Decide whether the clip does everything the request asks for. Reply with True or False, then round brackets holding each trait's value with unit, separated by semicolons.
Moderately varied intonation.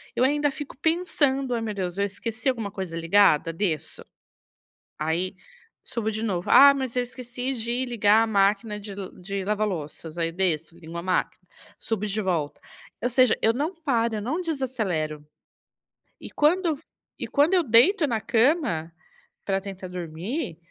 False (6.1 semitones)